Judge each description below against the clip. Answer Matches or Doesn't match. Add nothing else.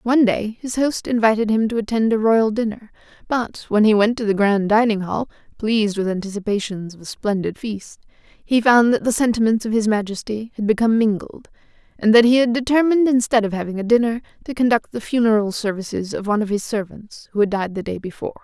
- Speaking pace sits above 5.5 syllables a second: Matches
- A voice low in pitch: Doesn't match